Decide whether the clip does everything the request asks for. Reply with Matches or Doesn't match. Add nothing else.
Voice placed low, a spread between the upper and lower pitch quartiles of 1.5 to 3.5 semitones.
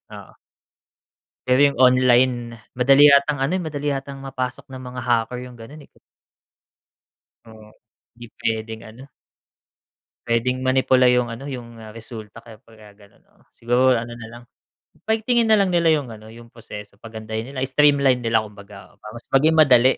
Matches